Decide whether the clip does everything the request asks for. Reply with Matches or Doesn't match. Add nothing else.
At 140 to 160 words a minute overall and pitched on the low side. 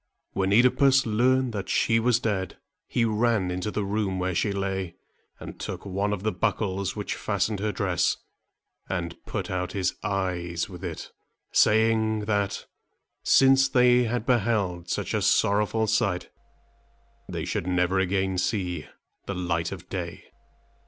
Matches